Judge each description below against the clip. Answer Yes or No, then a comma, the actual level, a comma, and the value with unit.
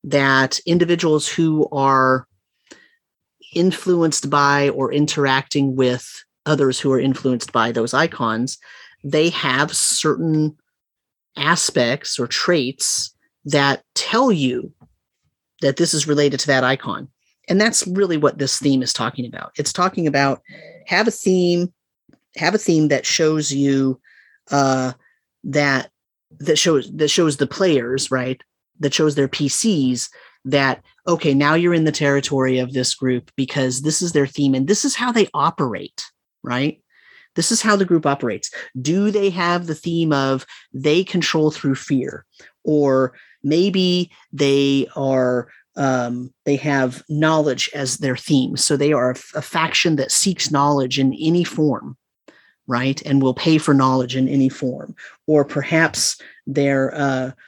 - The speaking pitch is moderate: Yes, medium, 145 Hz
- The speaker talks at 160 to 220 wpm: No, average, 145 wpm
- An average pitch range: Yes, average, 3.8 semitones